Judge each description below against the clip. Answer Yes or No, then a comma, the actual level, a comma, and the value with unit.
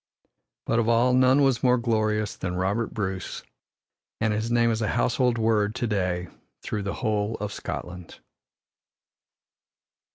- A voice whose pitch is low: Yes, low, 110 Hz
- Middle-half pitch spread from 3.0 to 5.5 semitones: No, narrow, 2.4 semitones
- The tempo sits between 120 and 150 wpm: Yes, average, 140 wpm